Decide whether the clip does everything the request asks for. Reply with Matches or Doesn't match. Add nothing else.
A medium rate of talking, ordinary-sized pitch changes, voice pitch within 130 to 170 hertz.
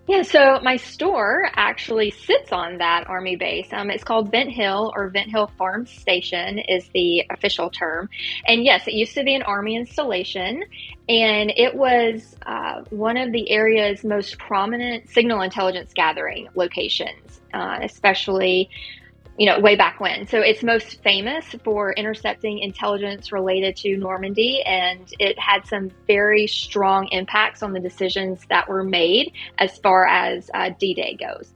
Doesn't match